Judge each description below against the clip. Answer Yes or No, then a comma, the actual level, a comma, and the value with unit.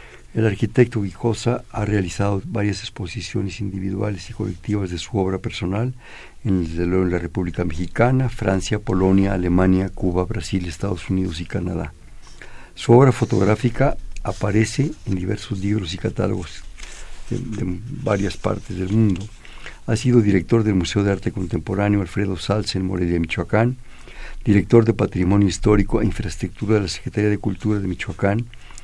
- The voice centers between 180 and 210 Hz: No, low, 100 Hz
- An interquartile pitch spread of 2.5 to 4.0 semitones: Yes, average, 3.3 semitones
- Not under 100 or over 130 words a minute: No, average, 145 wpm